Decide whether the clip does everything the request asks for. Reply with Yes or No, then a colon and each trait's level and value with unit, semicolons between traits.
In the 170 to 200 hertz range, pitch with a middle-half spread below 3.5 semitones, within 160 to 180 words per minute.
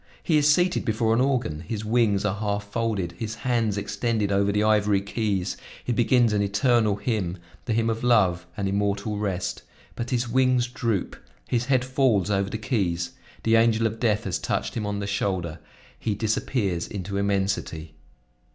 No: low, 105 Hz; average, 2.9 semitones; average, 175 wpm